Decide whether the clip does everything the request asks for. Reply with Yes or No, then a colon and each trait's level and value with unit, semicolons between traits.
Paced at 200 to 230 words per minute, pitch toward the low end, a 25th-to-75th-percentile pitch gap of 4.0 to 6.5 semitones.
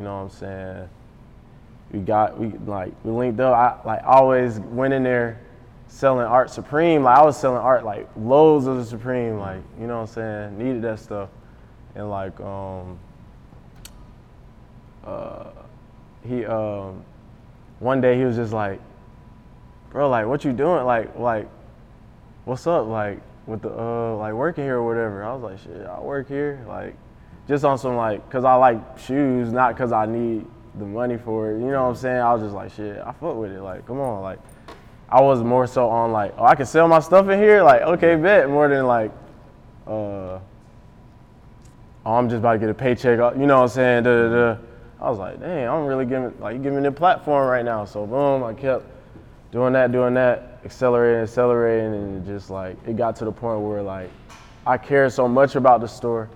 No: fast, 205 wpm; low, 120 Hz; average, 2.9 semitones